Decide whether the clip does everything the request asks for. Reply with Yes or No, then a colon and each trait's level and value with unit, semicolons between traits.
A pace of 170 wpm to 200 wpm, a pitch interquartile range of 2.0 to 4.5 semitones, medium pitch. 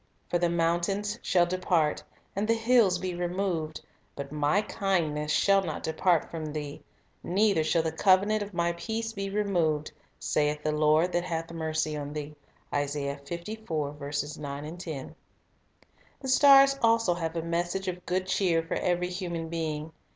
No: average, 150 wpm; average, 3.9 semitones; medium, 170 Hz